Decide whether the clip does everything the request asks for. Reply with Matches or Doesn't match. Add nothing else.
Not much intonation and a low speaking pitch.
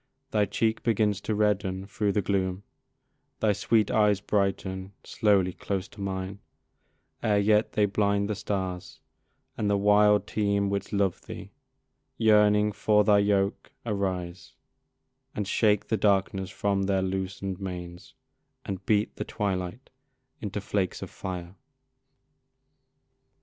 Matches